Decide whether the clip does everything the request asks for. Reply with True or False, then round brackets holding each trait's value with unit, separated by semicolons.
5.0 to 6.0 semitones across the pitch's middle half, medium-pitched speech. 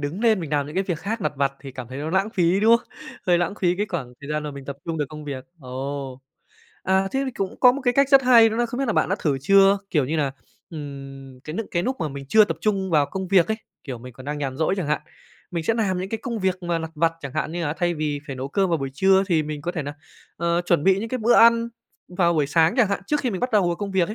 True (5.5 semitones; 170 Hz)